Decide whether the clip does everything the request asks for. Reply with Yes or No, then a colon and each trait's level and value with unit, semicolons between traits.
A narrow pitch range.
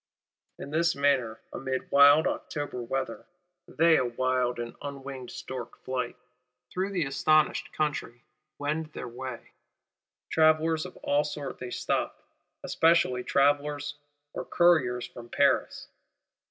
No: average, 3.4 semitones